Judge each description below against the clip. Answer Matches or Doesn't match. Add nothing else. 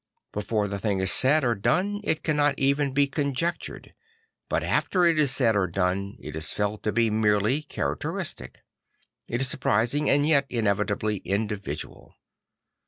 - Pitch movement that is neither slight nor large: Doesn't match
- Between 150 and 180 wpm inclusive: Matches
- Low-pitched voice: Matches